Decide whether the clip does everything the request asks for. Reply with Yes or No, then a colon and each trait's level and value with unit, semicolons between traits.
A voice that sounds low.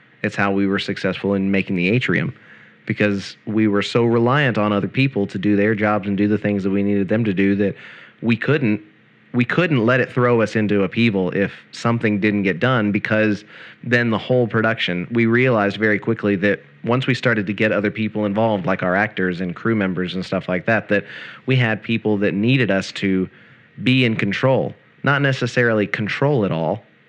Yes: low, 105 Hz